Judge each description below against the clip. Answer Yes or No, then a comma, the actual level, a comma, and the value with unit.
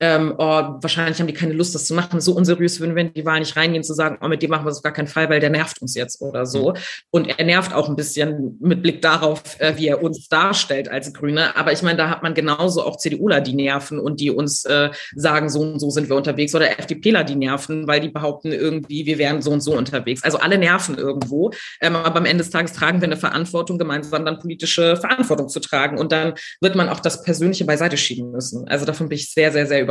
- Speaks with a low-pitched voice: No, medium, 155 Hz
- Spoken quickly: Yes, fast, 250 wpm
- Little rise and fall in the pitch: Yes, narrow, 2.1 semitones